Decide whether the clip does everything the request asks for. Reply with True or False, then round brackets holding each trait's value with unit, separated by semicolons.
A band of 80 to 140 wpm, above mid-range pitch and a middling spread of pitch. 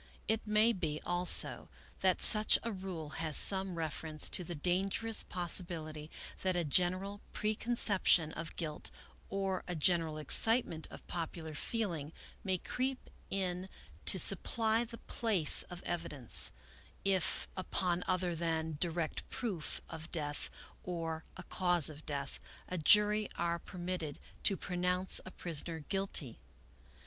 False (135 wpm; 175 Hz; 3.3 semitones)